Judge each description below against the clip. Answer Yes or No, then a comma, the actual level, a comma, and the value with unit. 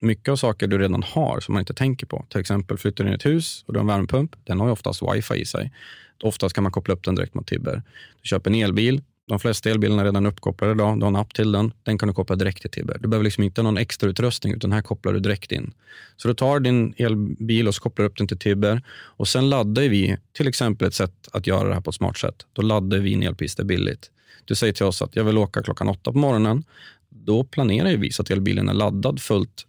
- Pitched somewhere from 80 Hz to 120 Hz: Yes, low, 105 Hz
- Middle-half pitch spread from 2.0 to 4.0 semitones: Yes, average, 3.2 semitones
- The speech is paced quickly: Yes, fast, 265 wpm